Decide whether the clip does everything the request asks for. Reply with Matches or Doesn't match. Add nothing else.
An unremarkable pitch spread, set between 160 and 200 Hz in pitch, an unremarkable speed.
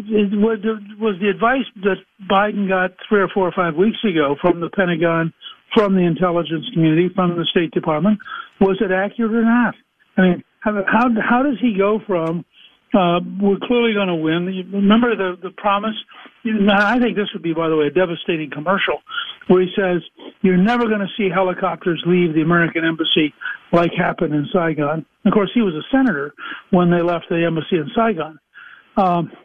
Matches